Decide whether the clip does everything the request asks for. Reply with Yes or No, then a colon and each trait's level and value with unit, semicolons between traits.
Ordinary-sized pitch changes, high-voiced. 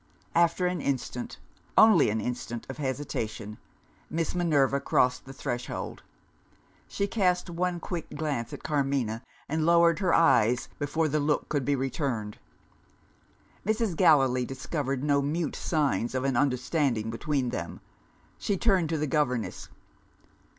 No: average, 4.7 semitones; medium, 145 Hz